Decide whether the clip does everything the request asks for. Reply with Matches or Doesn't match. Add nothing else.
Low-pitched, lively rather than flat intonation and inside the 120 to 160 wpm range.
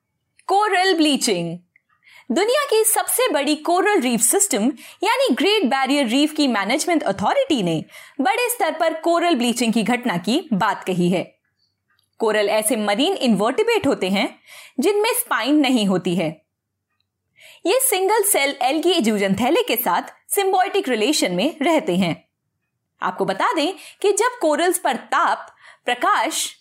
Doesn't match